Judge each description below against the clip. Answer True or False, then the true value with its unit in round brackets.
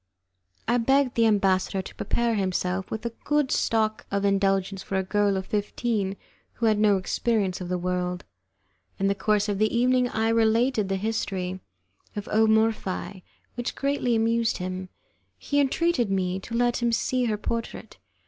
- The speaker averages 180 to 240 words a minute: False (165 wpm)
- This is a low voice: False (215 Hz)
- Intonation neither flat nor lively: True (3.3 semitones)